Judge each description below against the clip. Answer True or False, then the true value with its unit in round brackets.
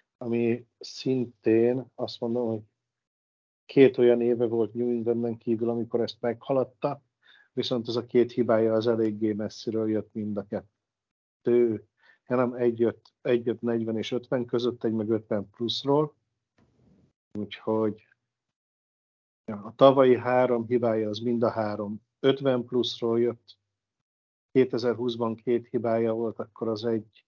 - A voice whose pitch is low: True (115 Hz)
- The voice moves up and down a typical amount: False (1.7 semitones)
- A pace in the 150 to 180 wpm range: False (130 wpm)